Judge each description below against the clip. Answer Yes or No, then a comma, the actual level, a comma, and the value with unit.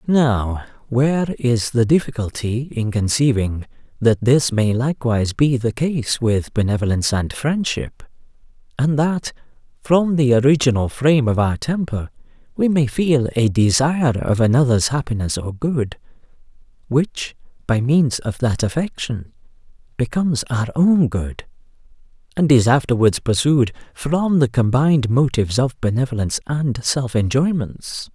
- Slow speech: Yes, slow, 130 wpm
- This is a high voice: No, low, 130 Hz